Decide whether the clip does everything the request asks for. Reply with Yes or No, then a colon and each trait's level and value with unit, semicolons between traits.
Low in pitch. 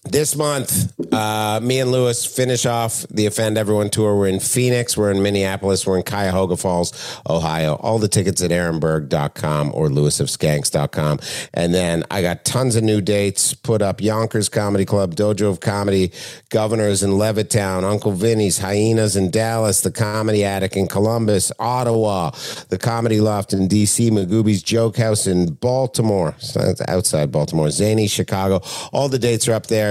Yes: low, 105 Hz